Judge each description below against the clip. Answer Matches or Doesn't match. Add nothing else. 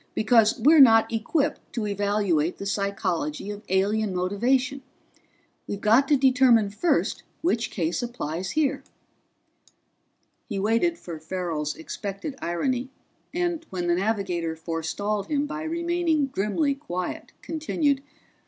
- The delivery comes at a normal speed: Doesn't match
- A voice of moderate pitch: Doesn't match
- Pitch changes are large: Matches